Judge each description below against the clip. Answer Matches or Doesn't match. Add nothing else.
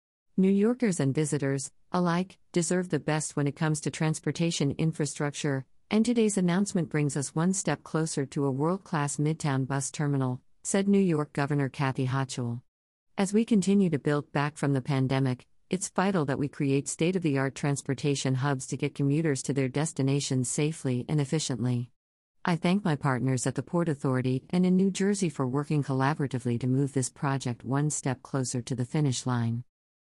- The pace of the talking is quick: Doesn't match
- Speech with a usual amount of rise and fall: Matches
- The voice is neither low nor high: Matches